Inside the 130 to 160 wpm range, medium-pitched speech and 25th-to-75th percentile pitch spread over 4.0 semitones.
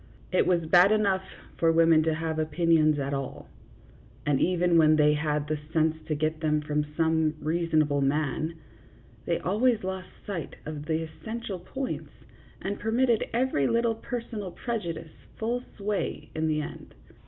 Yes: average, 155 wpm; medium, 165 Hz; average, 4.4 semitones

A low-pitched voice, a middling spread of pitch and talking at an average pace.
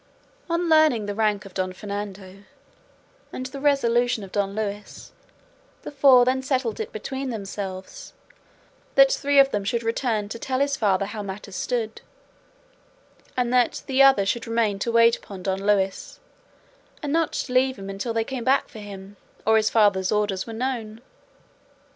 No: high, 225 Hz; average, 4.4 semitones; average, 165 wpm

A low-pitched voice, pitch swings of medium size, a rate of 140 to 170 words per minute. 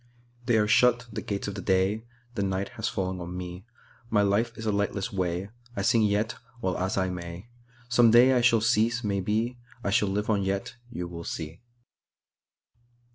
Yes: low, 105 Hz; average, 3.8 semitones; average, 165 wpm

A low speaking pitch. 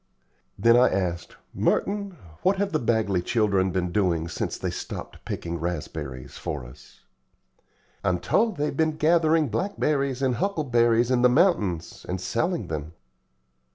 Yes: low, 120 Hz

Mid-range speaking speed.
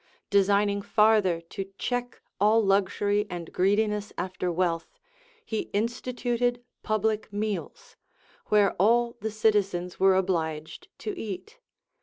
No: slow, 115 wpm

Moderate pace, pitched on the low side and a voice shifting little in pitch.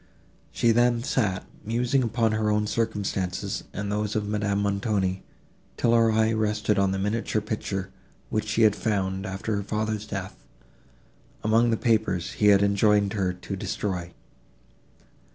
Yes: average, 150 wpm; low, 105 Hz; narrow, 2.0 semitones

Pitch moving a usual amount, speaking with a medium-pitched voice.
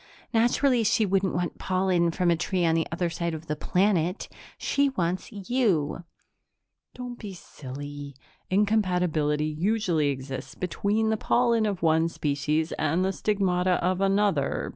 Yes: average, 4.5 semitones; medium, 180 Hz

